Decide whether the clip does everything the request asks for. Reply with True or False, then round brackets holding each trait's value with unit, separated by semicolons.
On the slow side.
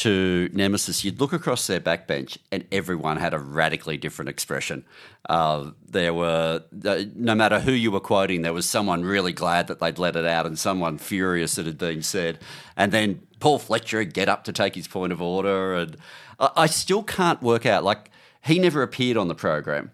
False (200 wpm)